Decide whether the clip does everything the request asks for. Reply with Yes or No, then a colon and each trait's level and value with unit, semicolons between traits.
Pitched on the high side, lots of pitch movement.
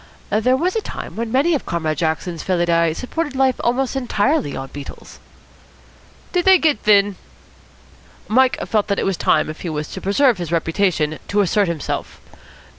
Yes: high, 200 Hz; wide, 7.6 semitones